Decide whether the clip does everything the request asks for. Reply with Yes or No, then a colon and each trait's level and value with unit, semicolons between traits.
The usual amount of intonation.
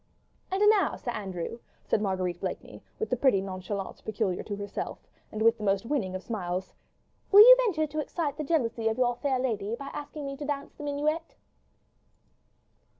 No: wide, 6.8 semitones